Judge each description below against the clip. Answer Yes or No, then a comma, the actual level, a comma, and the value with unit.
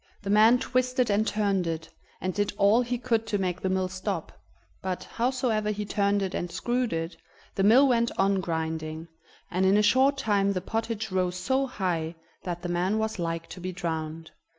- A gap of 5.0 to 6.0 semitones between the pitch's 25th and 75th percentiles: No, average, 4.0 semitones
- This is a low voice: No, high, 200 Hz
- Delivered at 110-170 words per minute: No, average, 195 wpm